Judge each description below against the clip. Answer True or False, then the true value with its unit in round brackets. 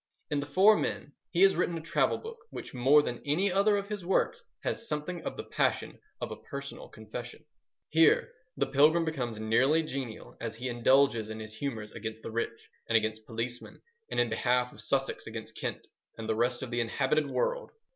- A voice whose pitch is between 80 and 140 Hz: True (135 Hz)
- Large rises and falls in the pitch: True (5.8 semitones)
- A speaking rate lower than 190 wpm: False (195 wpm)